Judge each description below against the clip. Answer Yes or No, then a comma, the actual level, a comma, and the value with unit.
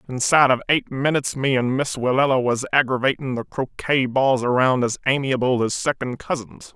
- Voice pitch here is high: No, low, 130 Hz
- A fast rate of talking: No, average, 170 wpm